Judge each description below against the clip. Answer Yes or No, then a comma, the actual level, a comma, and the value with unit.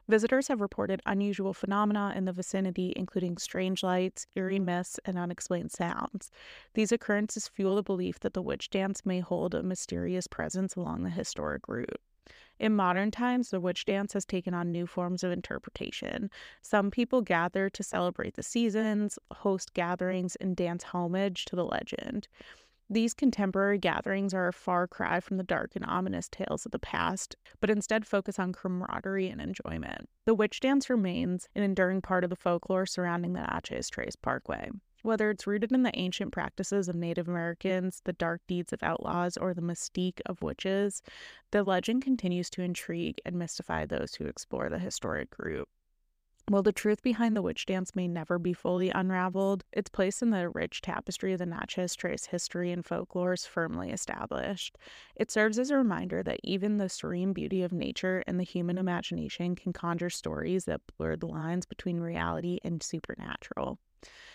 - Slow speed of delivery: No, average, 175 wpm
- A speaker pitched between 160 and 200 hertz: Yes, medium, 185 Hz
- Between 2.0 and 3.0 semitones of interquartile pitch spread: Yes, narrow, 2.6 semitones